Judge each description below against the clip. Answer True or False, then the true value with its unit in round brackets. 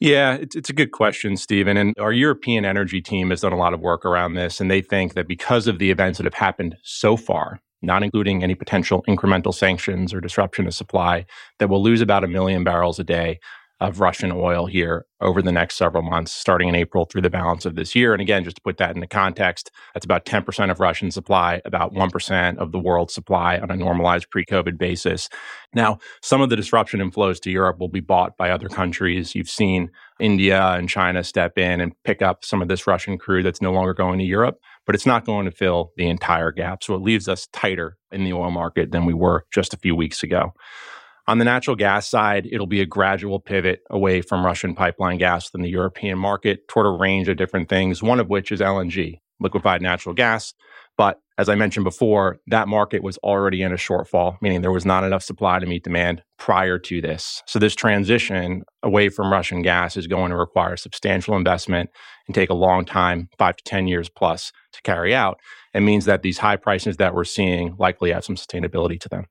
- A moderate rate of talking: False (220 wpm)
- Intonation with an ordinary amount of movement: False (2.1 semitones)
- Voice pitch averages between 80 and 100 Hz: True (95 Hz)